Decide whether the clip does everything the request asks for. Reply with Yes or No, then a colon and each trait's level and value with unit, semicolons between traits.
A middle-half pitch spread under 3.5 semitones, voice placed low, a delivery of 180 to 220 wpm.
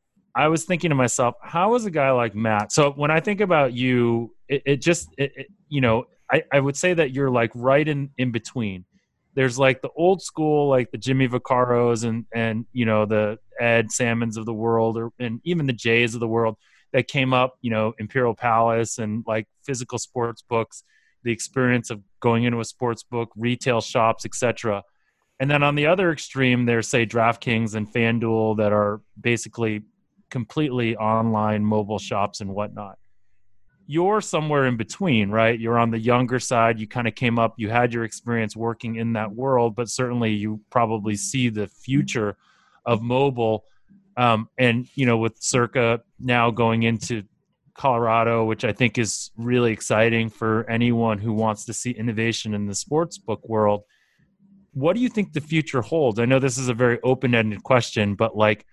Yes: average, 2.9 semitones; low, 120 Hz; average, 185 wpm